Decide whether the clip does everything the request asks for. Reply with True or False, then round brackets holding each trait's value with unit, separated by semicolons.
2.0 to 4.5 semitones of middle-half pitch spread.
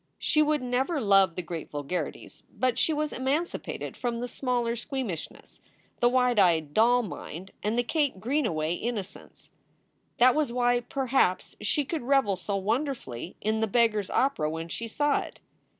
False (5.6 semitones)